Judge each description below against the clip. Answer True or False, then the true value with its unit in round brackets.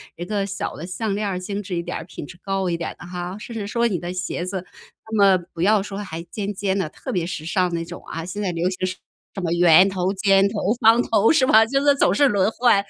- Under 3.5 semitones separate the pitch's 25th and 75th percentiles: True (2.8 semitones)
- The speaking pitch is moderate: False (195 Hz)